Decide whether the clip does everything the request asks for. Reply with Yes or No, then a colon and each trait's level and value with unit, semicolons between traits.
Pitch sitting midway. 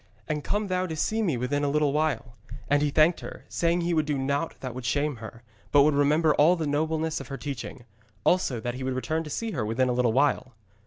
Yes: medium, 145 Hz